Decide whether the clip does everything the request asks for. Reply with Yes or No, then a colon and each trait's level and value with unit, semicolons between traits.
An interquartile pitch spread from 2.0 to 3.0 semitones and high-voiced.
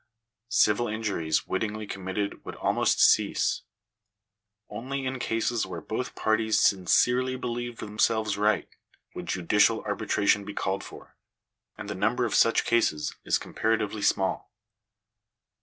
No: average, 2.7 semitones; low, 110 Hz